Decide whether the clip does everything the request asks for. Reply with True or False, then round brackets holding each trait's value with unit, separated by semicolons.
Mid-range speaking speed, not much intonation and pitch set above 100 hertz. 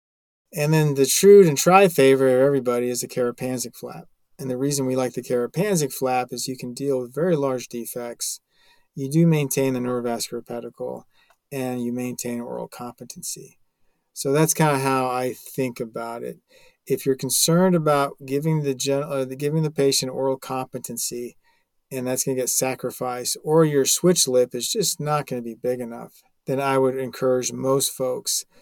True (175 wpm; 2.3 semitones; 130 Hz)